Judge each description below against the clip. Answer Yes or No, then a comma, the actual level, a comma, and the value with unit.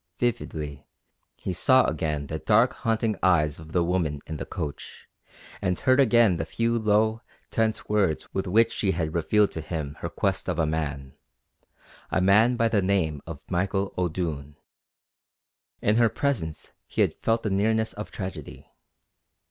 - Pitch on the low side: Yes, very low, 95 Hz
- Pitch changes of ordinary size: No, wide, 5.7 semitones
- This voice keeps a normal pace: Yes, average, 160 wpm